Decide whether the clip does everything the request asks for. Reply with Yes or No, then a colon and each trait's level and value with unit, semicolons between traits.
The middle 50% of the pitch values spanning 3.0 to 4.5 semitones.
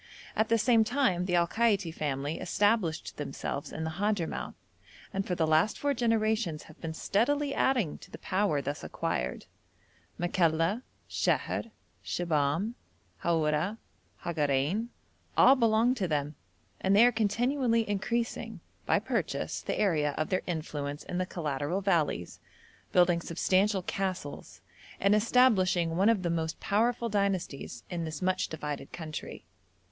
No: wide, 5.5 semitones